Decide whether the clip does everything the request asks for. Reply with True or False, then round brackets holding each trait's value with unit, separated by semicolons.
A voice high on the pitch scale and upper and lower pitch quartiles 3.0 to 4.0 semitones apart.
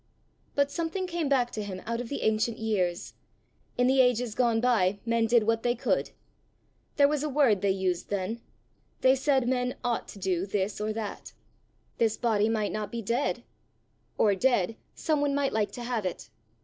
True (230 Hz; 3.7 semitones)